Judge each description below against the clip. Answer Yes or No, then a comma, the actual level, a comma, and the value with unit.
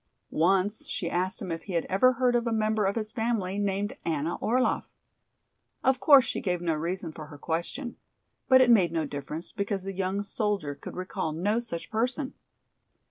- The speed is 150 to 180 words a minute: No, average, 190 wpm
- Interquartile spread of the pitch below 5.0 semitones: No, average, 5.3 semitones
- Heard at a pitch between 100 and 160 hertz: No, high, 195 Hz